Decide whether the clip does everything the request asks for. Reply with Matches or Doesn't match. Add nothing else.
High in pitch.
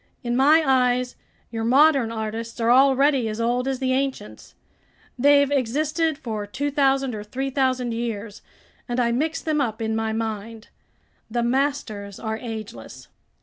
Matches